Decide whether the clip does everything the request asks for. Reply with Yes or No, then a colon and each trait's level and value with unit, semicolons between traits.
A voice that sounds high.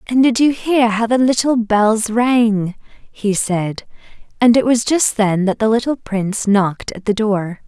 Yes: high, 220 Hz